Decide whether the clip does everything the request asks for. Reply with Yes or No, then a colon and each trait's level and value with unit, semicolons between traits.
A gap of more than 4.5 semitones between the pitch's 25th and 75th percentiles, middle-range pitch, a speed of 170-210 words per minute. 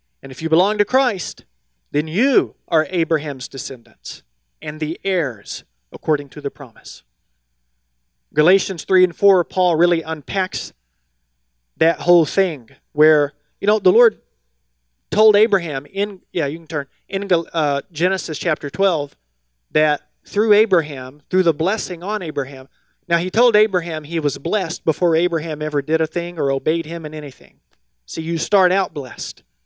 No: average, 5.1 semitones; medium, 160 Hz; average, 155 wpm